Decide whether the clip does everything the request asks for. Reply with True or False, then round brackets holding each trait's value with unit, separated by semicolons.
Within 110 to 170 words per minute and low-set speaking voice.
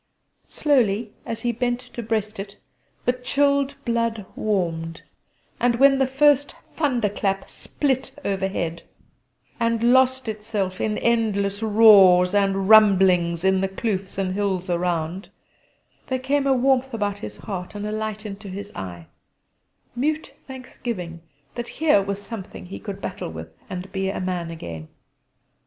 False (140 wpm; 210 Hz)